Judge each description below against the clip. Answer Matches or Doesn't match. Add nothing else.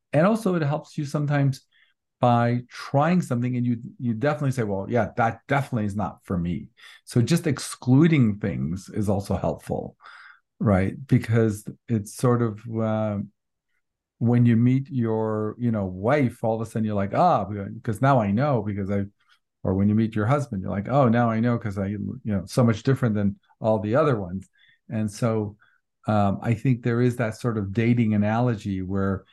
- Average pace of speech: Matches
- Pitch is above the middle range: Doesn't match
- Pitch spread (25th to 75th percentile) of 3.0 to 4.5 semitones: Matches